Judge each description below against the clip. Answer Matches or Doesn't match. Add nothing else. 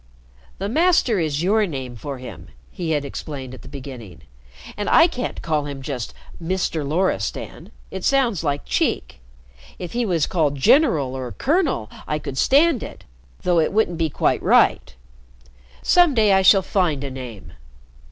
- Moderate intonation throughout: Doesn't match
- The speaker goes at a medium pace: Matches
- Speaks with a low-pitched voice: Doesn't match